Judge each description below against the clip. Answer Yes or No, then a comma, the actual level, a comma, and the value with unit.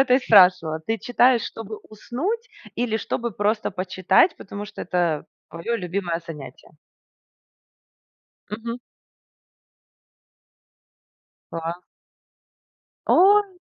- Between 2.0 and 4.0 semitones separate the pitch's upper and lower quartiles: No, average, 5.3 semitones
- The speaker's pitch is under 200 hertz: No, high, 210 Hz